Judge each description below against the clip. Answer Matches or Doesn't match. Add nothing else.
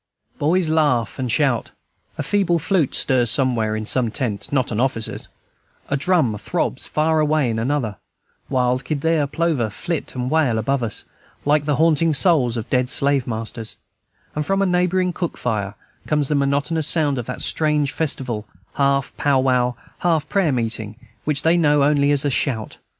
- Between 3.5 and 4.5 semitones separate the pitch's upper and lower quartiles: Matches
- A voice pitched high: Doesn't match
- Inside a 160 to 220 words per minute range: Matches